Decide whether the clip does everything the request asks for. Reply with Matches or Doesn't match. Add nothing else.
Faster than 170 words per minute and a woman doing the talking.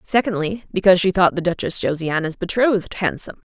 Doesn't match